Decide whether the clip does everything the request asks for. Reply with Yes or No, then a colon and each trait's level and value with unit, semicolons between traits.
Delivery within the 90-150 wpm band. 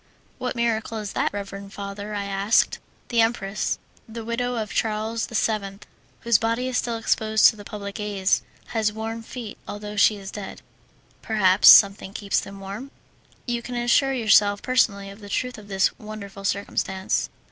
No: average, 165 wpm